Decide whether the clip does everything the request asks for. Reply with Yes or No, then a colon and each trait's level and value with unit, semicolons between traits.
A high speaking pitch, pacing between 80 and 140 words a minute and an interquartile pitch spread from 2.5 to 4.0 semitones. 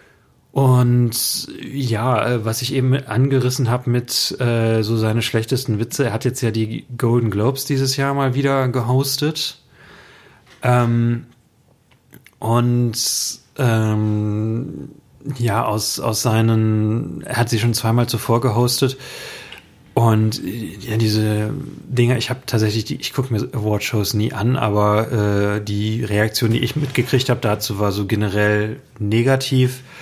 No: low, 120 Hz; average, 130 wpm; average, 2.9 semitones